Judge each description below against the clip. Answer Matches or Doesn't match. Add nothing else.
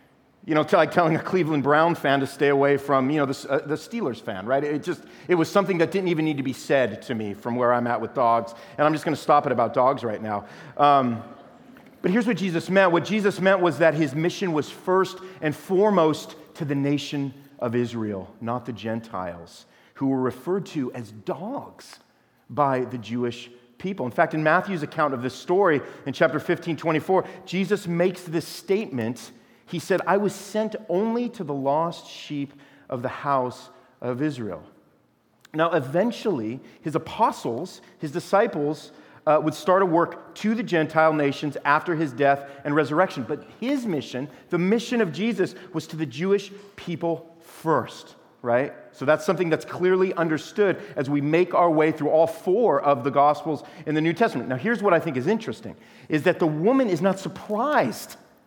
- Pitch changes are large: Doesn't match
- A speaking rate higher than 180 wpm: Matches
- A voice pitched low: Doesn't match